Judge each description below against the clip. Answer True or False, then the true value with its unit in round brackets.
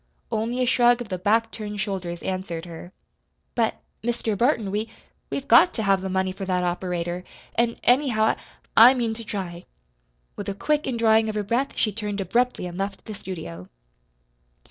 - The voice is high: True (210 Hz)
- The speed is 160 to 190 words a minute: True (180 wpm)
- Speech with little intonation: False (3.9 semitones)